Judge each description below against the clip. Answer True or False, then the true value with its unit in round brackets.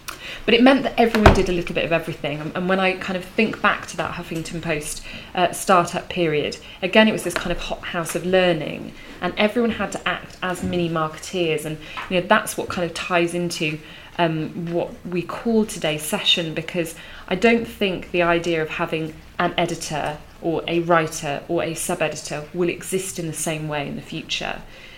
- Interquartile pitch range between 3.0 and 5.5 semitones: False (2.4 semitones)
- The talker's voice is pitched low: False (175 Hz)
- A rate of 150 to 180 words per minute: False (200 wpm)